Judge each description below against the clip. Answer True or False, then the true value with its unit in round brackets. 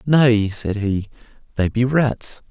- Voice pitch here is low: True (115 Hz)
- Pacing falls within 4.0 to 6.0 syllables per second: False (3.2 syllables/s)